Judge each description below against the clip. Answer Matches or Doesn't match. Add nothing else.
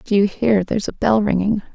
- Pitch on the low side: Doesn't match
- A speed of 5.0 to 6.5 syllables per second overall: Matches